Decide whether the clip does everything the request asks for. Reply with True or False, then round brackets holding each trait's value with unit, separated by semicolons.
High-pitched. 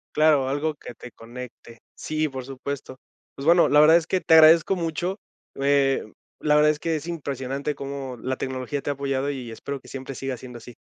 False (140 Hz)